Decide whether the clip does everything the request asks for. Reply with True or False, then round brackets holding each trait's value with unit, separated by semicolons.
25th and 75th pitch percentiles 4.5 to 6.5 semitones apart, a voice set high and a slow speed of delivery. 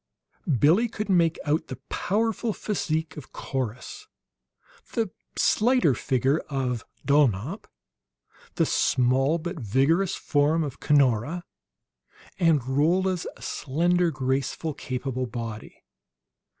False (5.2 semitones; 150 Hz; 100 wpm)